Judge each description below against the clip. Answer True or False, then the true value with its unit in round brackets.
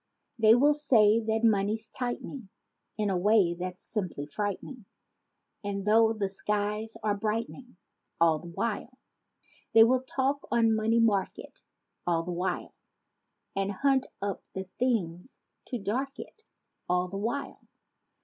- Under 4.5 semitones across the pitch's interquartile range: True (3.5 semitones)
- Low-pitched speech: False (215 Hz)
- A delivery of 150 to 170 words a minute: False (135 wpm)